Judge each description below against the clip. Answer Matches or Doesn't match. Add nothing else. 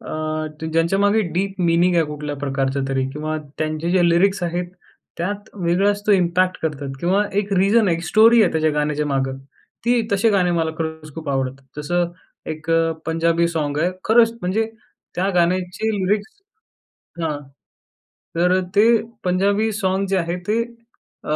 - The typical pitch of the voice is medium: Matches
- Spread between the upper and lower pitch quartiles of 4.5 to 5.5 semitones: Doesn't match